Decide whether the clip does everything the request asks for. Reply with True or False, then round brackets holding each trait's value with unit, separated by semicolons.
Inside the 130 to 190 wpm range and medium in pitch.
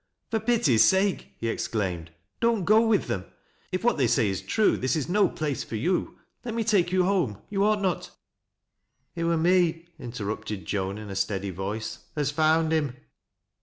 False (200 wpm; 160 Hz)